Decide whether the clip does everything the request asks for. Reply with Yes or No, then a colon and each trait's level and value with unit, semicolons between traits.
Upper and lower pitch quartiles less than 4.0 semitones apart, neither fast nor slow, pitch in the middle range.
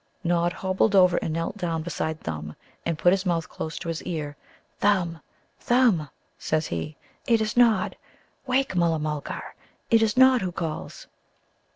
No: average, 4.5 semitones; average, 160 wpm; medium, 175 Hz